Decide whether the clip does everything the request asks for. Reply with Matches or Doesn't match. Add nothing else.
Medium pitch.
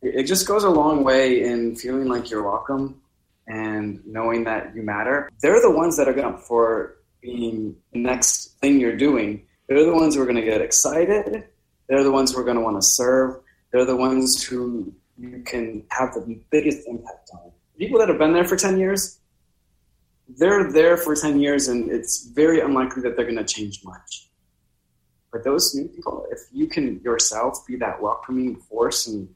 Doesn't match